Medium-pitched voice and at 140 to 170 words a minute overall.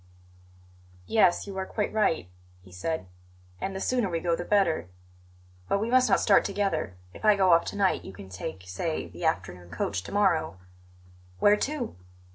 No: medium, 180 Hz; average, 180 wpm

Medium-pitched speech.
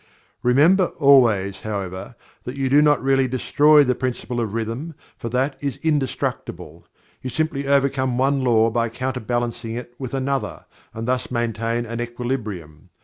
No: low, 125 Hz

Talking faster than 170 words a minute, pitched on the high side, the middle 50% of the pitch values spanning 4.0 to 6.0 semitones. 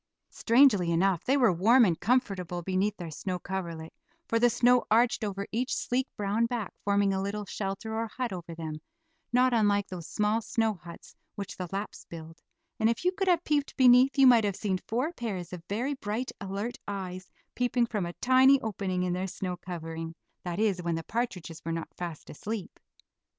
Yes: average, 190 wpm; high, 205 Hz; average, 4.9 semitones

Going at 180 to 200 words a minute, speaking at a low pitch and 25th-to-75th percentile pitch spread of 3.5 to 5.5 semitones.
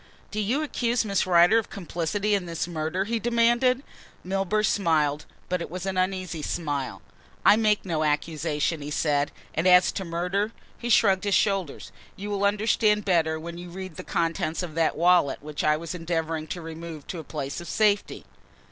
No: average, 185 wpm; medium, 180 Hz; average, 4.1 semitones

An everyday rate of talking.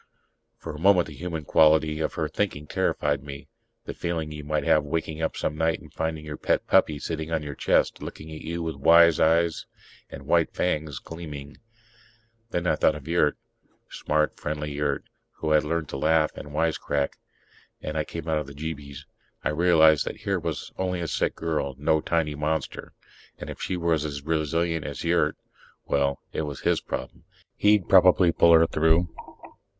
Yes: average, 185 wpm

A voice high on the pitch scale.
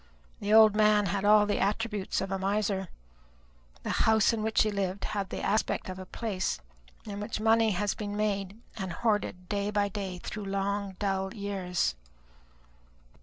Yes: high, 205 Hz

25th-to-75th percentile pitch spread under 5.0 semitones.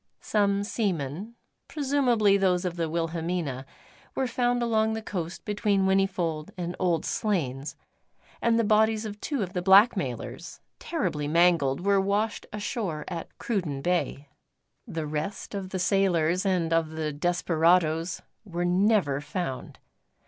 Yes: average, 4.2 semitones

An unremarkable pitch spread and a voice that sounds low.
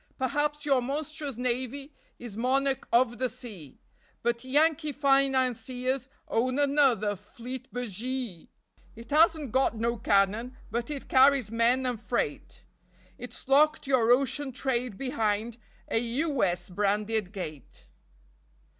No: average, 3.4 semitones; very high, 250 Hz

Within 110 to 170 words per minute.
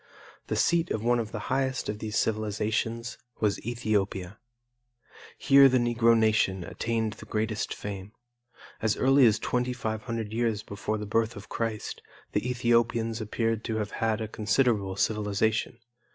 Yes: average, 145 wpm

